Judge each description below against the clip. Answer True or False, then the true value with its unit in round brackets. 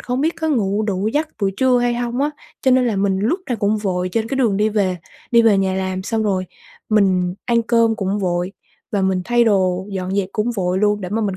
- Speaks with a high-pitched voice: True (210 Hz)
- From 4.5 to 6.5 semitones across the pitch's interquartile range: False (3.8 semitones)